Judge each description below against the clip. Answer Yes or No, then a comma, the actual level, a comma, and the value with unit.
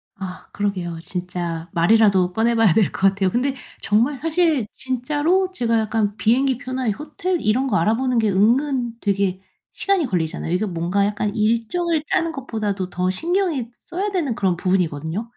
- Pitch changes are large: Yes, wide, 6.0 semitones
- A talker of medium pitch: No, high, 220 Hz